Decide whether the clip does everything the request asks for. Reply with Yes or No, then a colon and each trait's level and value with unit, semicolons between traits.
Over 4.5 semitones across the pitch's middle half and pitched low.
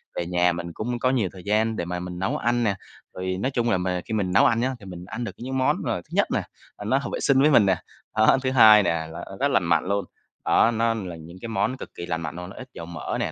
Yes: average, 5.1 semitones; low, 100 Hz